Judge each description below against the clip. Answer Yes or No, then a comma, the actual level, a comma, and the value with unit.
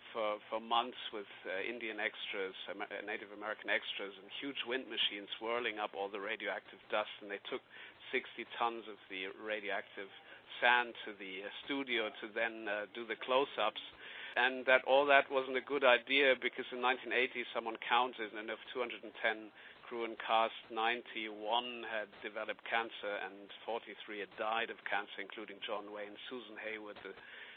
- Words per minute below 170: Yes, average, 160 wpm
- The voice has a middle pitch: No, low, 115 Hz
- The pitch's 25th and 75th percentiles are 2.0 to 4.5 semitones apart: Yes, average, 3.0 semitones